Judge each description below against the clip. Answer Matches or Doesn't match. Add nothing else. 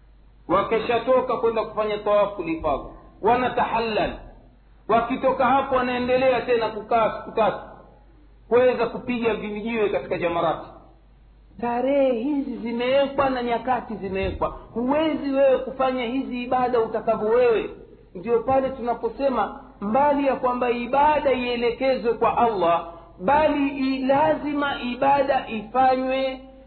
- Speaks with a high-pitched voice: Matches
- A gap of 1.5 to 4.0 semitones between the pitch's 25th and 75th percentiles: Matches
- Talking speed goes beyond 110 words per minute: Doesn't match